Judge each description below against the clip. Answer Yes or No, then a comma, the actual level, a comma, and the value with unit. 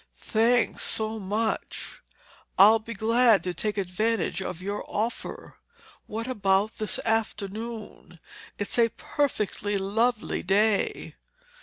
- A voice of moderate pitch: No, high, 215 Hz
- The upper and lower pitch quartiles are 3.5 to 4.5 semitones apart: No, narrow, 2.4 semitones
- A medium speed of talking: No, slow, 110 wpm